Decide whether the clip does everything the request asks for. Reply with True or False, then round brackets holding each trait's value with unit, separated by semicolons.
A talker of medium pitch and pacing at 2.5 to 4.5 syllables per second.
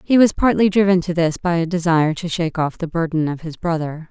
False (170 Hz; 6.1 syllables/s)